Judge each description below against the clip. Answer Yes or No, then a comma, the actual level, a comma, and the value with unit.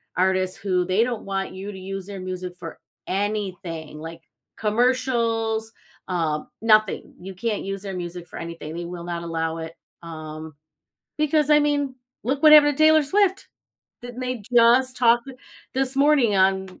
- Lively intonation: Yes, wide, 6.0 semitones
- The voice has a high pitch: Yes, high, 195 Hz